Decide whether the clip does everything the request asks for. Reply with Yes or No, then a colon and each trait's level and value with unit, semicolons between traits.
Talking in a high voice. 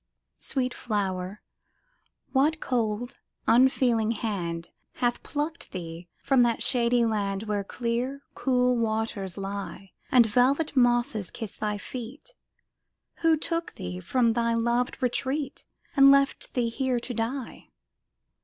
Yes: high, 235 Hz